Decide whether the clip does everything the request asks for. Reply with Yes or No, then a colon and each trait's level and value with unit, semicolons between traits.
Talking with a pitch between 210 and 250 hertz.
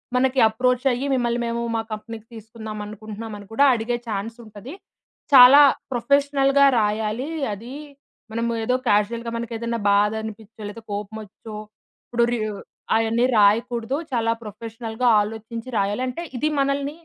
Yes: high, 230 Hz